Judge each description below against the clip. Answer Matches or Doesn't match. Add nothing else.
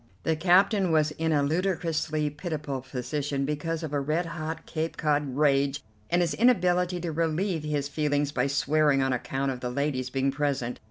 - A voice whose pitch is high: Doesn't match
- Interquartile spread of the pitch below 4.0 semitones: Matches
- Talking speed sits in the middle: Matches